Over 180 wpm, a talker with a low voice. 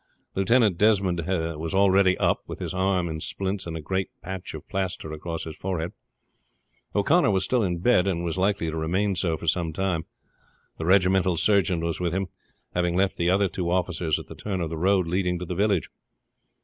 Yes: average, 200 wpm; very low, 90 Hz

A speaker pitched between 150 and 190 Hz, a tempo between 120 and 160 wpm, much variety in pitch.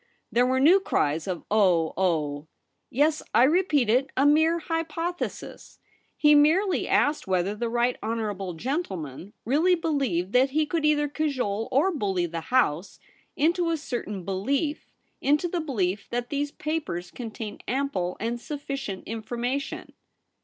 No: very high, 255 Hz; average, 155 wpm; wide, 7.2 semitones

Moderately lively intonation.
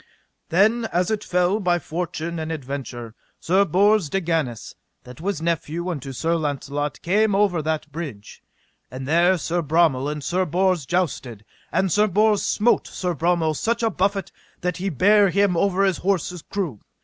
Yes: average, 4.2 semitones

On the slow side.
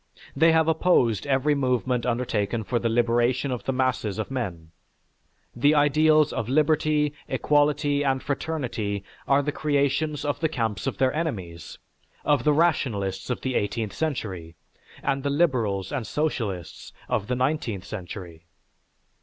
No: average, 145 wpm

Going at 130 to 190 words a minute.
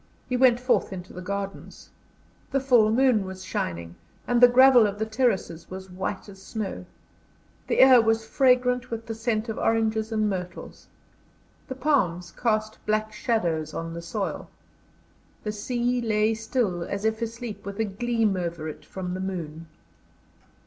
Yes: average, 160 wpm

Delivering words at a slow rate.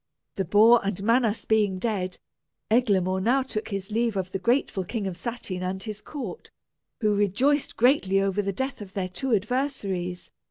No: average, 170 wpm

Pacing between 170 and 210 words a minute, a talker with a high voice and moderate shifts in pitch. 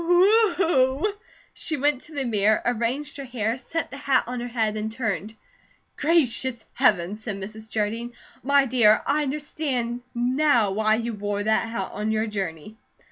No: average, 160 wpm; high, 240 Hz; average, 4.5 semitones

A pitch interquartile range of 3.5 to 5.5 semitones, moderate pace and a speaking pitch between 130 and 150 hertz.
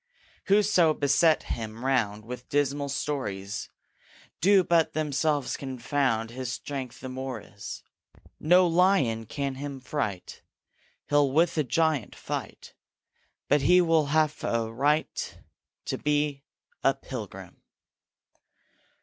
No: average, 3.8 semitones; slow, 115 wpm; medium, 140 Hz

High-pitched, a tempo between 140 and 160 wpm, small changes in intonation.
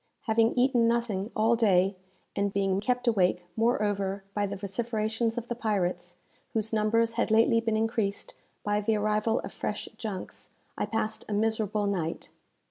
Yes: high, 215 Hz; average, 155 wpm; narrow, 2.2 semitones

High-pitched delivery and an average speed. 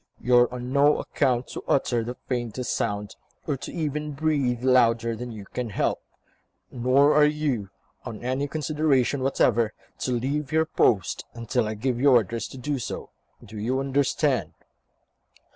No: low, 125 Hz; average, 160 wpm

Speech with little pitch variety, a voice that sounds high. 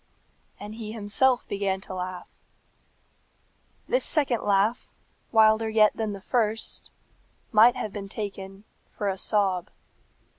Yes: narrow, 2.2 semitones; high, 210 Hz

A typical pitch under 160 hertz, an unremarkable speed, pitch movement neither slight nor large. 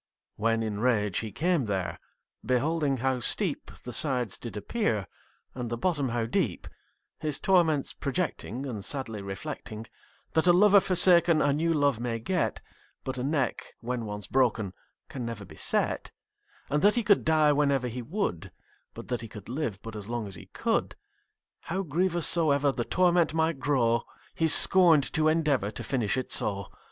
No: low, 135 Hz; average, 170 wpm; wide, 5.8 semitones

